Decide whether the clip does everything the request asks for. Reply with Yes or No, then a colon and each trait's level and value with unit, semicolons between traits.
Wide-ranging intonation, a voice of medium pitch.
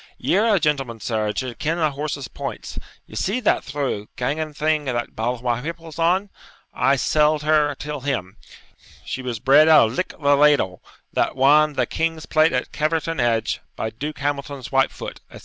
No: average, 3.7 semitones; medium, 145 Hz